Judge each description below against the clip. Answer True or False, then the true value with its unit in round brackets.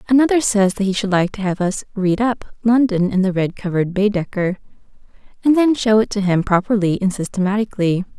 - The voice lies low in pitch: False (200 Hz)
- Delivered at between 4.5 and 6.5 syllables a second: True (5.8 syllables/s)